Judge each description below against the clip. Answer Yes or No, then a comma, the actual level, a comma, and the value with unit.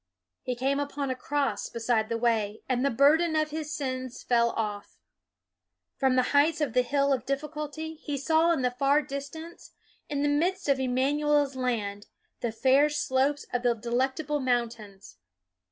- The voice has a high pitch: Yes, very high, 270 Hz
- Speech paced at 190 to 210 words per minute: No, average, 165 wpm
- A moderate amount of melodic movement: Yes, average, 3.3 semitones